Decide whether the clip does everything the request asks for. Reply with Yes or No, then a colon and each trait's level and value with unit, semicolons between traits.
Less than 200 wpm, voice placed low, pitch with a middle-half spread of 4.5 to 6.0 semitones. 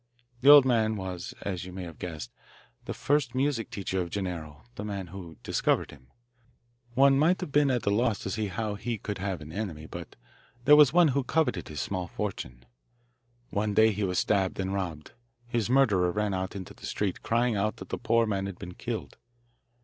No: fast, 205 wpm; low, 100 Hz; average, 4.8 semitones